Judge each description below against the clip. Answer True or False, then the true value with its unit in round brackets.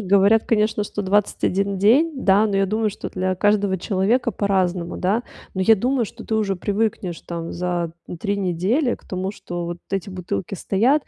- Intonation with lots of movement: False (2.7 semitones)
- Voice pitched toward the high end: True (200 Hz)